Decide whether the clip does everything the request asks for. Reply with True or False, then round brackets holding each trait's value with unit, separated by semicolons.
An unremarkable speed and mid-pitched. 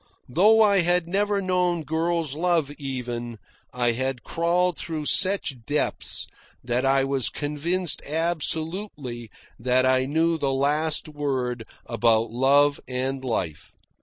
False (125 wpm; 145 Hz)